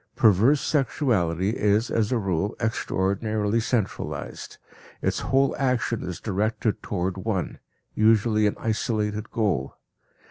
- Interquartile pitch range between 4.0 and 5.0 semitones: No, average, 2.7 semitones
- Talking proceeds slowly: Yes, slow, 110 wpm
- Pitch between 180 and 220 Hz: No, low, 110 Hz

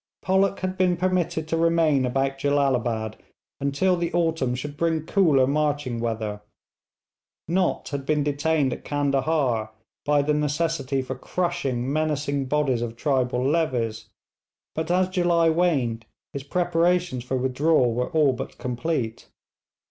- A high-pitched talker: No, medium, 145 Hz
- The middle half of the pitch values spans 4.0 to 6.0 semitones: Yes, average, 4.3 semitones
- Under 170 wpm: Yes, slow, 135 wpm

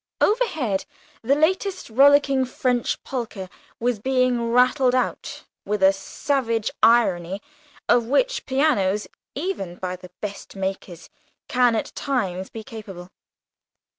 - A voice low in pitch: No, high, 240 Hz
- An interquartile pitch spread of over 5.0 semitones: Yes, wide, 5.6 semitones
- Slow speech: Yes, slow, 115 wpm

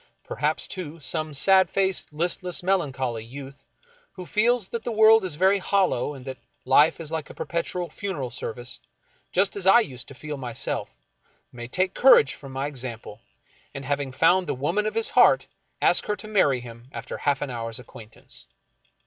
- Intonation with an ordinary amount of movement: No, wide, 6.5 semitones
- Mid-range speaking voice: Yes, medium, 150 Hz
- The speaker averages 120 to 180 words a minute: Yes, average, 175 wpm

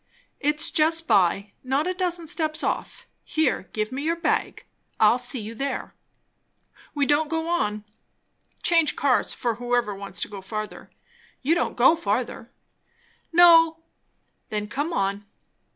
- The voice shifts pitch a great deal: Yes, wide, 7.3 semitones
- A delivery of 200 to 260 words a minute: No, average, 140 wpm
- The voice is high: Yes, very high, 275 Hz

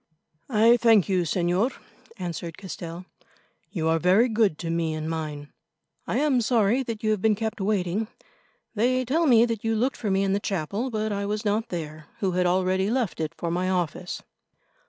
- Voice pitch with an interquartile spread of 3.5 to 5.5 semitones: Yes, average, 4.4 semitones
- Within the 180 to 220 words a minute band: Yes, average, 190 wpm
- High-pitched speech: Yes, high, 200 Hz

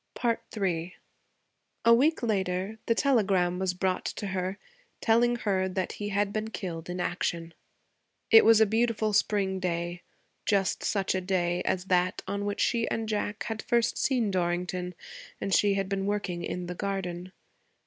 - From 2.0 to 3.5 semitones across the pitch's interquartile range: Yes, average, 3.0 semitones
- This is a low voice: No, high, 195 Hz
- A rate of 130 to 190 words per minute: Yes, average, 160 wpm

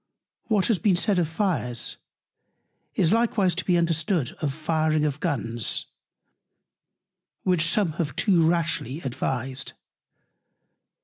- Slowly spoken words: Yes, slow, 115 wpm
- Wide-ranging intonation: No, average, 4.3 semitones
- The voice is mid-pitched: Yes, medium, 165 Hz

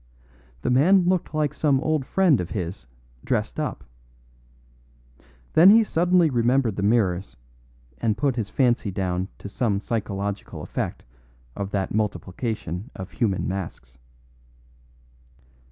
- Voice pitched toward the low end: Yes, low, 110 Hz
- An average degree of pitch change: No, wide, 6.7 semitones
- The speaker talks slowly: Yes, slow, 120 wpm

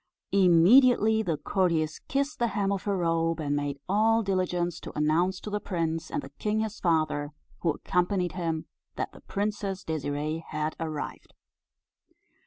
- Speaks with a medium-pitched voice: Yes, medium, 175 Hz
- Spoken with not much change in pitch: No, average, 4.3 semitones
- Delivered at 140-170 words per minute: Yes, average, 155 wpm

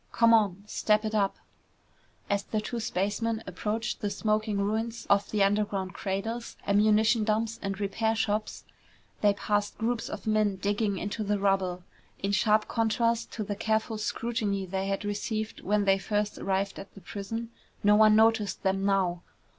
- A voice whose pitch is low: No, high, 210 Hz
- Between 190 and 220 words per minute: No, average, 160 wpm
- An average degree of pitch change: No, narrow, 1.8 semitones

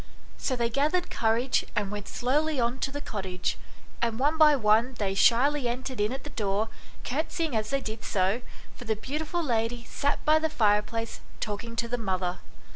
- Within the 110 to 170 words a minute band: No, average, 185 wpm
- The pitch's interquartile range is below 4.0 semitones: No, average, 4.6 semitones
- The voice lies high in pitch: Yes, high, 235 Hz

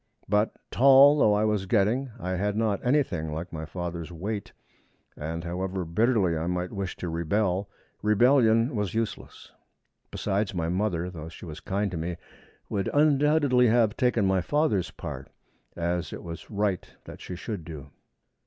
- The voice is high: No, low, 100 Hz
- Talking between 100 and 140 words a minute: No, average, 160 wpm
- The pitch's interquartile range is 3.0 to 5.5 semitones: Yes, average, 4.5 semitones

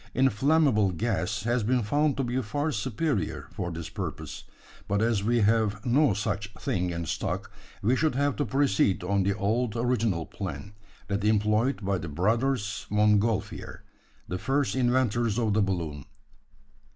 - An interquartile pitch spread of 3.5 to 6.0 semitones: Yes, average, 4.1 semitones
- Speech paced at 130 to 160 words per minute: Yes, average, 150 wpm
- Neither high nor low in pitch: No, low, 110 Hz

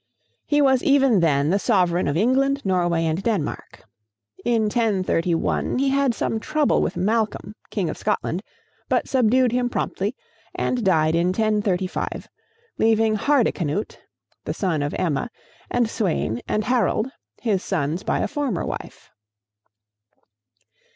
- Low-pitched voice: No, high, 210 Hz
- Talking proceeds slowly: Yes, slow, 130 wpm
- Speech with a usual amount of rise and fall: No, wide, 5.7 semitones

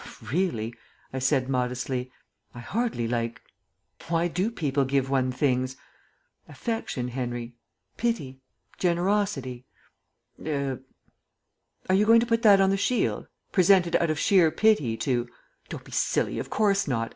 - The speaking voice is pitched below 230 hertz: Yes, medium, 140 Hz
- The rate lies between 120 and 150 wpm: Yes, average, 145 wpm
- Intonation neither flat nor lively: No, wide, 7.5 semitones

